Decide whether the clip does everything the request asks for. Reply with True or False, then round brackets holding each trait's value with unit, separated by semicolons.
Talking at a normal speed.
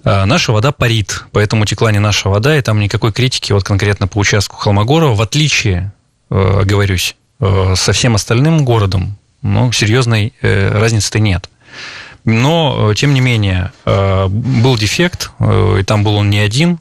True (145 wpm)